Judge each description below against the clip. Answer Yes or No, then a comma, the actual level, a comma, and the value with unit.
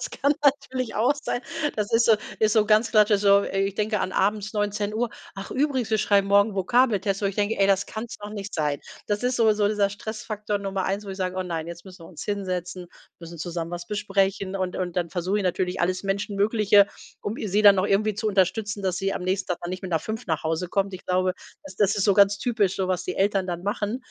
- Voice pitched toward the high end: Yes, high, 200 Hz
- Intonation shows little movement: Yes, narrow, 2.3 semitones